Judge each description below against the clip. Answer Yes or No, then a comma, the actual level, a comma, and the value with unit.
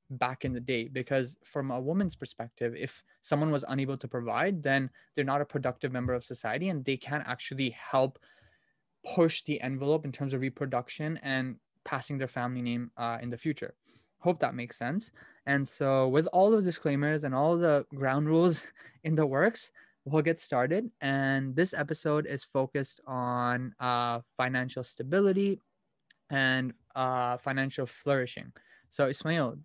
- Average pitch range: Yes, average, 3.2 semitones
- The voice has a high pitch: No, low, 135 Hz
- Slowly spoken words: No, average, 160 wpm